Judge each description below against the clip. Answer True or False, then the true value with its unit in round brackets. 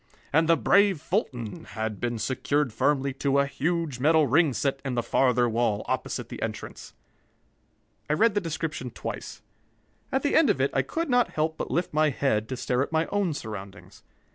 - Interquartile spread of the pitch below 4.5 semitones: False (4.9 semitones)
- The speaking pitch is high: False (140 Hz)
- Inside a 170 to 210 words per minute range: True (190 wpm)